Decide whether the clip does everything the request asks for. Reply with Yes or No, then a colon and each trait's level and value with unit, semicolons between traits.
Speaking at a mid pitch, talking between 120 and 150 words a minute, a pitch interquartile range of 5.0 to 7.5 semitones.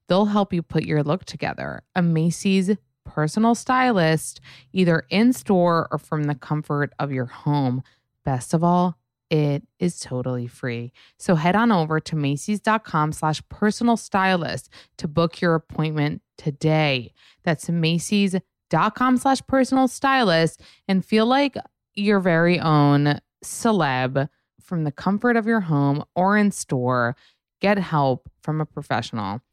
Yes: medium, 160 Hz; slow, 135 wpm; wide, 5.5 semitones